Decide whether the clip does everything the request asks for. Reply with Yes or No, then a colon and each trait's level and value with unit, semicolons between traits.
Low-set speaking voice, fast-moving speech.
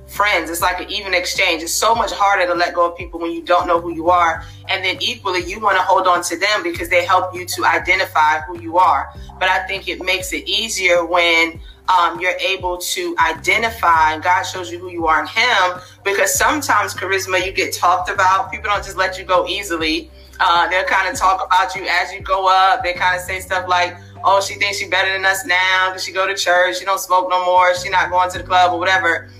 No: medium, 180 Hz; fast, 245 wpm